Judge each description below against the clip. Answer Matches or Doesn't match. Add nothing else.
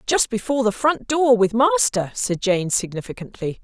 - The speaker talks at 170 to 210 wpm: Doesn't match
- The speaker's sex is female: Matches